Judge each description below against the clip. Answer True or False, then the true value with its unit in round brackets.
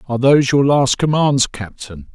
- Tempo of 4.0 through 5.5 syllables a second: True (5.1 syllables/s)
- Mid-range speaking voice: False (130 Hz)